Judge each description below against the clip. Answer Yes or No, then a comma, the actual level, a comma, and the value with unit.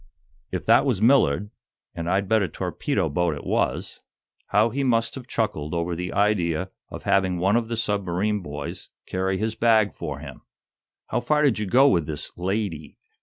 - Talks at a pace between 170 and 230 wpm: Yes, average, 180 wpm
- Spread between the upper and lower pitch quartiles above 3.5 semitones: Yes, average, 4.2 semitones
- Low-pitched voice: Yes, low, 100 Hz